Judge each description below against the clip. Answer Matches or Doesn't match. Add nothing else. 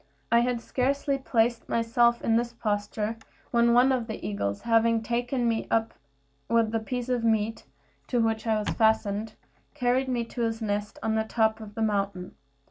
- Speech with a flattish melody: Matches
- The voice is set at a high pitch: Matches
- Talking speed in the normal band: Matches